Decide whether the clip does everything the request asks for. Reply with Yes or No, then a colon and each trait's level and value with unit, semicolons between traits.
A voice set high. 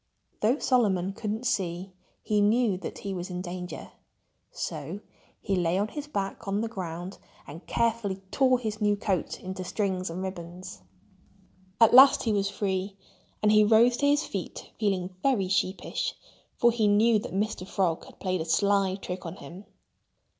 Yes: high, 195 Hz